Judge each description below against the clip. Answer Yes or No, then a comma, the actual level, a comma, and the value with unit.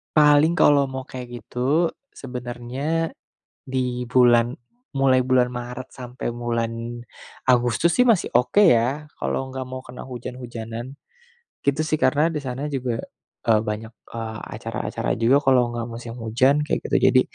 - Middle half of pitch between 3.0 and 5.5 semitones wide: No, narrow, 2.5 semitones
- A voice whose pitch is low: Yes, low, 125 Hz